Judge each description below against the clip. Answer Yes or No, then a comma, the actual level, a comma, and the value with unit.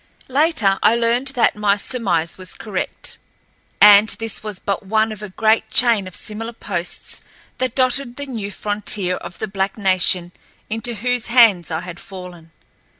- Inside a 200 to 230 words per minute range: No, average, 160 wpm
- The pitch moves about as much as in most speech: Yes, average, 3.7 semitones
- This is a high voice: Yes, high, 210 Hz